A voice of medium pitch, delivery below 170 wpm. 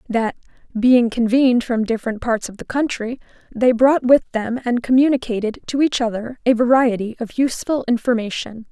No: high, 240 Hz; average, 160 wpm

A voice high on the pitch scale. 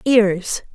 Yes: high, 210 Hz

